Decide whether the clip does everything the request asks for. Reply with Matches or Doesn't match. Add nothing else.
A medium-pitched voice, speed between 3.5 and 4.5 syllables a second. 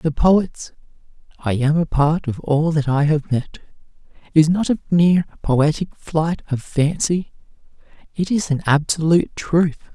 Matches